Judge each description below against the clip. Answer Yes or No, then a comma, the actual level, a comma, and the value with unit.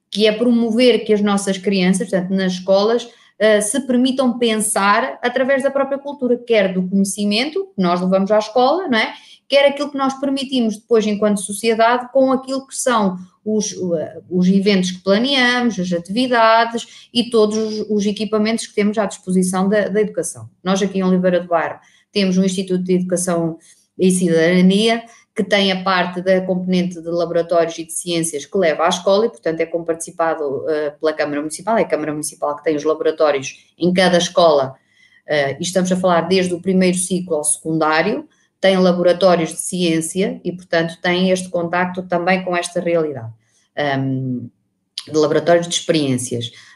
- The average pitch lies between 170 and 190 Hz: Yes, medium, 185 Hz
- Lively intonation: No, average, 4.3 semitones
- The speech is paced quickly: No, average, 165 wpm